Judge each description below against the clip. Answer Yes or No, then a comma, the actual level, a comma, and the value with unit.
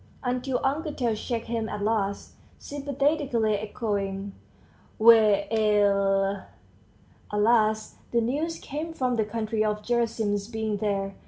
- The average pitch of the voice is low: No, high, 220 Hz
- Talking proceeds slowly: Yes, slow, 120 wpm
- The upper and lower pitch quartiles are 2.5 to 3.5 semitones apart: Yes, average, 3.0 semitones